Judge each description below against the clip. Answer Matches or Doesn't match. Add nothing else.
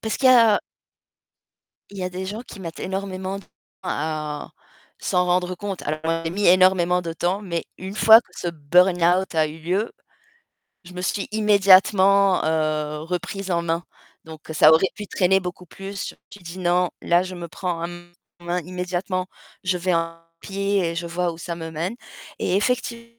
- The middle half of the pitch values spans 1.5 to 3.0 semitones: Matches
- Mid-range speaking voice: Matches